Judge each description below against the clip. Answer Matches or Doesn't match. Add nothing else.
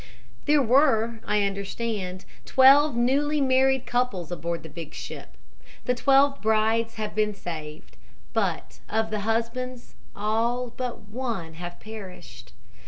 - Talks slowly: Matches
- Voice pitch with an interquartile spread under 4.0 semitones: Doesn't match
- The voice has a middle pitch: Doesn't match